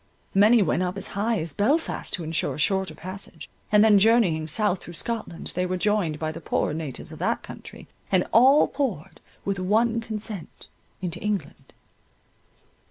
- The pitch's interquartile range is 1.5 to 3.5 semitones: No, average, 4.4 semitones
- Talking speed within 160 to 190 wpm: Yes, average, 165 wpm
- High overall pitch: Yes, high, 195 Hz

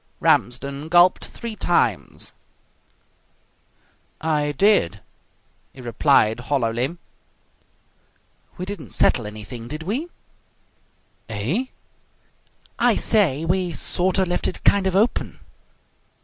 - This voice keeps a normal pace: No, slow, 95 wpm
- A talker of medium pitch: Yes, medium, 155 Hz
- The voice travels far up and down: Yes, wide, 7.5 semitones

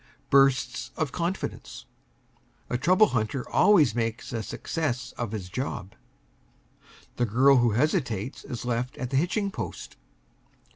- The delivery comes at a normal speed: No, slow, 130 wpm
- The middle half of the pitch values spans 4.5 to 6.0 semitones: Yes, average, 4.8 semitones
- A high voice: No, low, 125 Hz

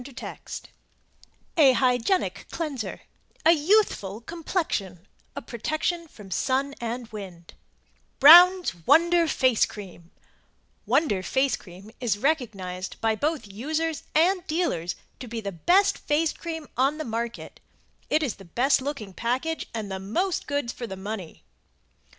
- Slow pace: Yes, slow, 130 wpm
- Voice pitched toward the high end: Yes, very high, 255 Hz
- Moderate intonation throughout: No, wide, 7.7 semitones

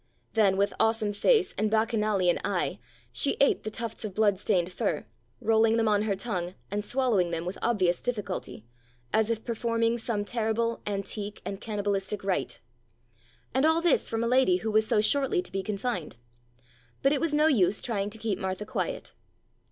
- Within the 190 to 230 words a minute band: No, average, 175 wpm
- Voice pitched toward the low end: No, high, 215 Hz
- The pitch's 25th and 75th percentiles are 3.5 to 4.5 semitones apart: No, average, 2.8 semitones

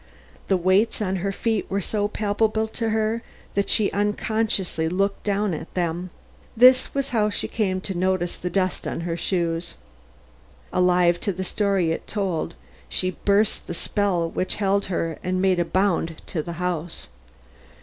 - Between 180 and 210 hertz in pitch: Yes, high, 190 Hz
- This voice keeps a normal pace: Yes, average, 165 wpm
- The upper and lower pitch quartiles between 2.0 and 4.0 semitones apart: Yes, average, 3.0 semitones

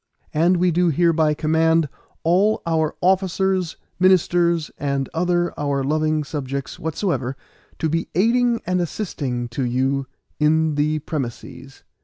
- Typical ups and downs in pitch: Yes, average, 3.5 semitones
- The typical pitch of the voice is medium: Yes, medium, 160 Hz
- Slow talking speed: Yes, slow, 125 wpm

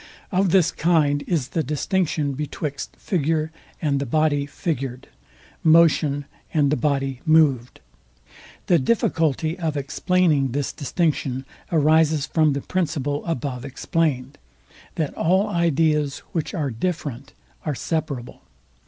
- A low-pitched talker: No, medium, 150 Hz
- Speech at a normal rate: No, slow, 120 wpm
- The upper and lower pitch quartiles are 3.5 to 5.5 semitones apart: No, average, 2.9 semitones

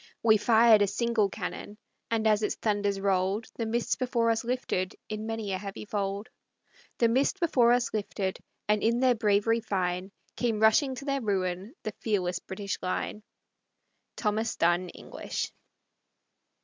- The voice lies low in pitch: No, high, 215 Hz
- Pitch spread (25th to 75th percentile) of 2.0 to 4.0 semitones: Yes, average, 2.8 semitones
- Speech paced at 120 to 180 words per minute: Yes, average, 150 wpm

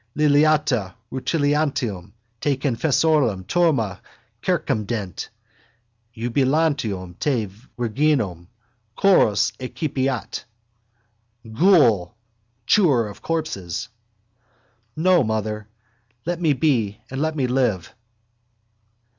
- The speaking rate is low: Yes, slow, 75 wpm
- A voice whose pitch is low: Yes, low, 130 Hz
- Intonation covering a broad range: Yes, wide, 6.2 semitones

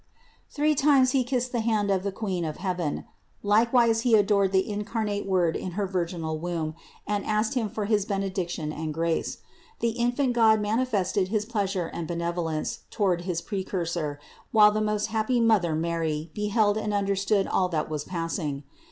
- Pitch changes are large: No, average, 4.2 semitones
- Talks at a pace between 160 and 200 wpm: Yes, average, 170 wpm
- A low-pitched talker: No, high, 200 Hz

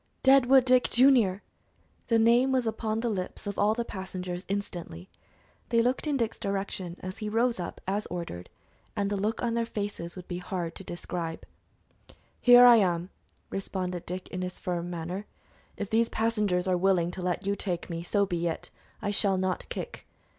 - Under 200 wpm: Yes, average, 185 wpm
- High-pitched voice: Yes, high, 195 Hz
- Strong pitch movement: No, average, 4.1 semitones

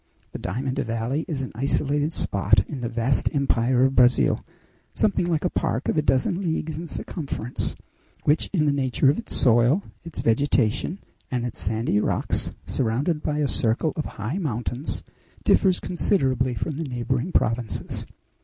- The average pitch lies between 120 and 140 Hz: Yes, low, 135 Hz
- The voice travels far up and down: No, average, 4.5 semitones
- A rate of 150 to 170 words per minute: Yes, average, 160 wpm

